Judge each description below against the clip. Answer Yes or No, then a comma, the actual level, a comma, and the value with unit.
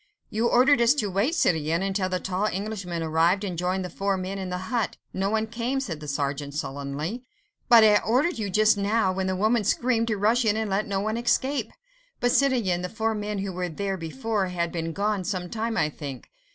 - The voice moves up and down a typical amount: Yes, average, 3.8 semitones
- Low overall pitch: No, high, 200 Hz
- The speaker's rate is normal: No, fast, 220 wpm